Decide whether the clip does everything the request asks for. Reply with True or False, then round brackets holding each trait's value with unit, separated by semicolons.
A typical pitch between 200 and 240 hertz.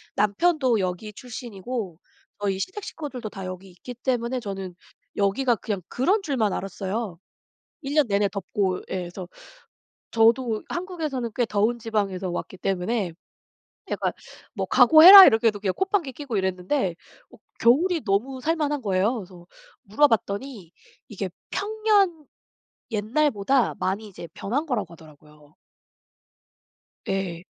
True (220 Hz)